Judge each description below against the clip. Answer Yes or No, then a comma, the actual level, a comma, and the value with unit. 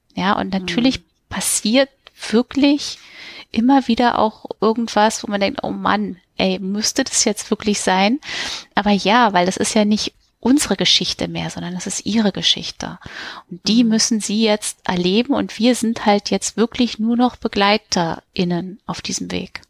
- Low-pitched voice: No, high, 215 Hz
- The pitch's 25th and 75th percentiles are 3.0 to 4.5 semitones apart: Yes, average, 3.6 semitones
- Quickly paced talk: No, average, 160 wpm